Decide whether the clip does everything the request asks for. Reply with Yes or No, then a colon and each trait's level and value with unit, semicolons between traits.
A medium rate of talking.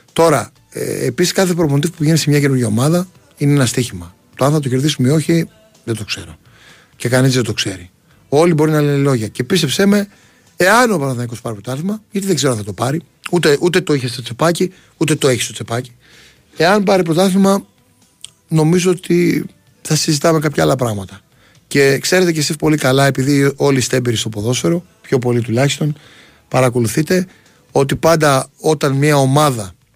No: fast, 180 wpm